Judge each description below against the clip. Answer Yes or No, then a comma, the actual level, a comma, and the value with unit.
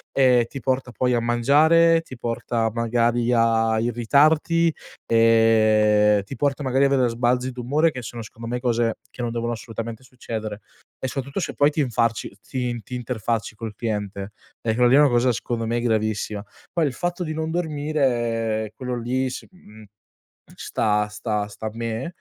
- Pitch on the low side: Yes, low, 120 Hz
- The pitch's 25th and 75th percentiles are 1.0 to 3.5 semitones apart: Yes, average, 2.8 semitones